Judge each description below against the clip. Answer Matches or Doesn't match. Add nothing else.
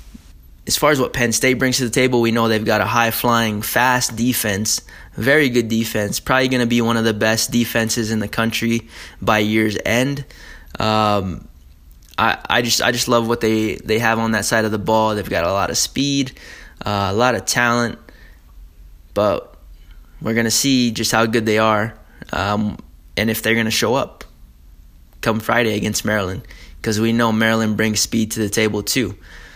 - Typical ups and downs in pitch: Doesn't match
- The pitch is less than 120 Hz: Matches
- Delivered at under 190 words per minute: Doesn't match